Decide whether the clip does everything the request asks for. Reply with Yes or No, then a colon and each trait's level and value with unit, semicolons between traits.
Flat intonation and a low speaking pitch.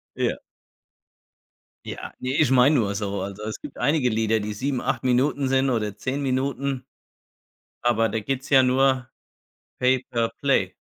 No: average, 3.2 semitones; low, 125 Hz